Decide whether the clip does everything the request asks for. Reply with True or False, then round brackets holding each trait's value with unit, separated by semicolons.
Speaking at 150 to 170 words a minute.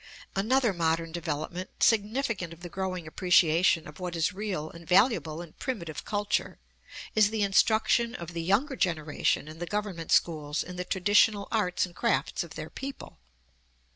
True (160 wpm)